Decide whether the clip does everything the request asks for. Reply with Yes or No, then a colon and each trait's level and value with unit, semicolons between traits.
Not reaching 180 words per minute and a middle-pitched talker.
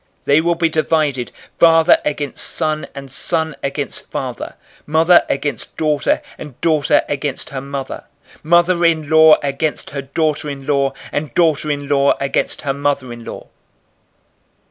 Yes: average, 150 wpm; medium, 150 Hz